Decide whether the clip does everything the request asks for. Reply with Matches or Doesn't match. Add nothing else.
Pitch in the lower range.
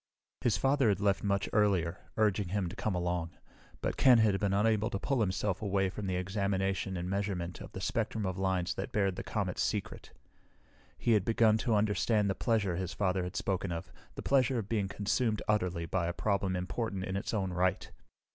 Matches